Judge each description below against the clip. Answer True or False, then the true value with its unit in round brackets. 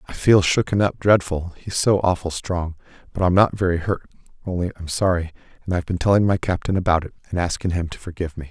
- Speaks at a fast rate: True (220 wpm)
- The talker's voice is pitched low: True (90 Hz)